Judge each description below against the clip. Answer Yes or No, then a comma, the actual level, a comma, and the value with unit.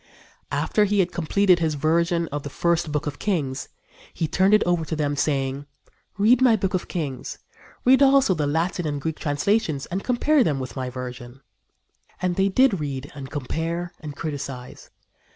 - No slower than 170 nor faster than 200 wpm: Yes, average, 175 wpm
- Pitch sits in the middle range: Yes, medium, 160 Hz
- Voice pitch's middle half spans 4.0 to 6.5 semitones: Yes, average, 5.1 semitones